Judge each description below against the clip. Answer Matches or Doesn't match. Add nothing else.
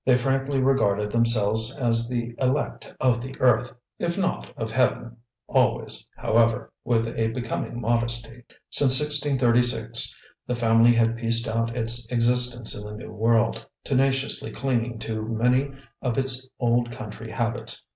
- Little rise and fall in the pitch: Matches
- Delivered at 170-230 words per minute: Doesn't match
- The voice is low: Matches